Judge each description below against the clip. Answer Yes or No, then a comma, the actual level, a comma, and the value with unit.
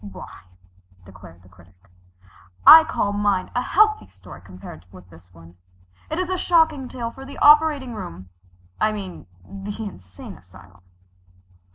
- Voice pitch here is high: Yes, high, 195 Hz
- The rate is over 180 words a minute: No, average, 145 wpm